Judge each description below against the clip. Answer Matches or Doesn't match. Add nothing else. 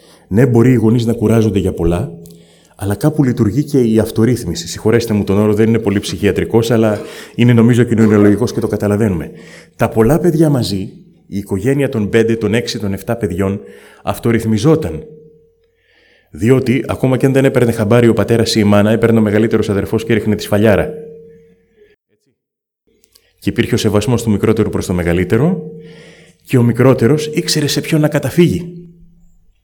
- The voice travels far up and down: Matches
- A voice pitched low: Matches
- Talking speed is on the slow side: Doesn't match